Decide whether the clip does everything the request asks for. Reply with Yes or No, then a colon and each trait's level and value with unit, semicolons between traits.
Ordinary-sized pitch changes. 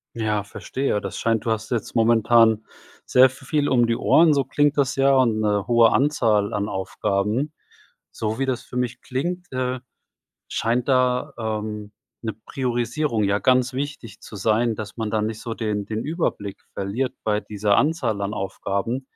Yes: average, 3.5 semitones